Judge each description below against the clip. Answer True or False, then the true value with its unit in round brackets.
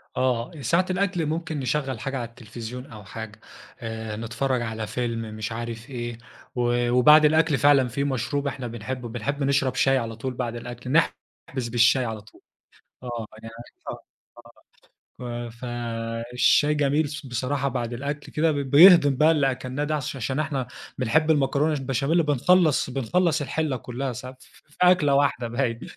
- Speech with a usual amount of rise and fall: True (3.5 semitones)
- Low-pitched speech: True (130 Hz)